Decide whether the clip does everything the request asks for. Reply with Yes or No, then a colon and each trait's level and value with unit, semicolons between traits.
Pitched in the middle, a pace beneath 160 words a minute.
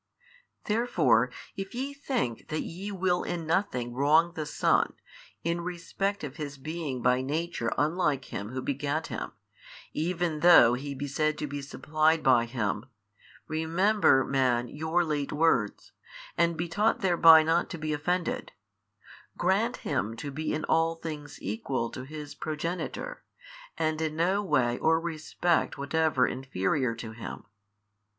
Yes: medium, 155 Hz; average, 145 wpm